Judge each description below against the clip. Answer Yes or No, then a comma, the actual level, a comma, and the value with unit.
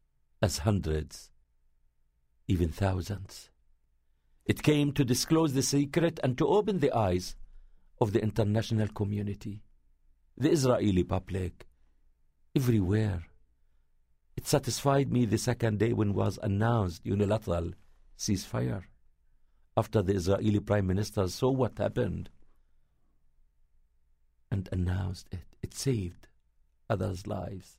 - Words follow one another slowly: Yes, slow, 105 wpm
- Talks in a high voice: No, very low, 95 Hz